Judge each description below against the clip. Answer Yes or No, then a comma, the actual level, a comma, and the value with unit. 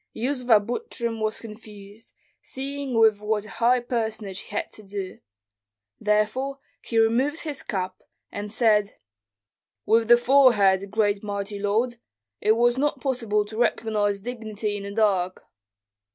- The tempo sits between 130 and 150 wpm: Yes, average, 140 wpm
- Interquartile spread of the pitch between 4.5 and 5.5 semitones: No, average, 2.8 semitones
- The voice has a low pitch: No, high, 220 Hz